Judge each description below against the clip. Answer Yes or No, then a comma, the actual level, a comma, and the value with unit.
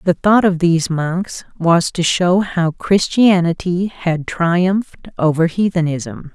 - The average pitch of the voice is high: No, medium, 175 Hz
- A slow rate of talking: Yes, slow, 130 wpm